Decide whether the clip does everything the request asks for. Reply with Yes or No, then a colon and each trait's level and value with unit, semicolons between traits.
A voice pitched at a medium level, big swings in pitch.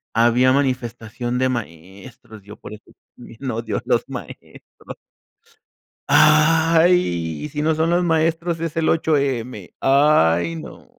No: low, 130 Hz; wide, 6.3 semitones